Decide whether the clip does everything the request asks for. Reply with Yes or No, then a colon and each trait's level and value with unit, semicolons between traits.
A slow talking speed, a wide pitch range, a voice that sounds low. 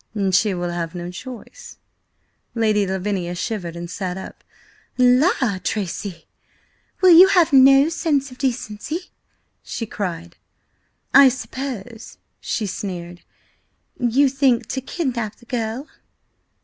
No: slow, 115 wpm; wide, 6.4 semitones; high, 230 Hz